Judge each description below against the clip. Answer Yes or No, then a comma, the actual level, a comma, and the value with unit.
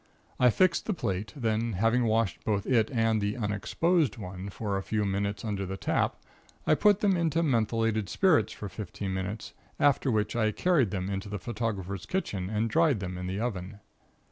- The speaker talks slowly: No, average, 185 wpm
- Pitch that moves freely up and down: No, average, 3.8 semitones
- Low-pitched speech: Yes, low, 110 Hz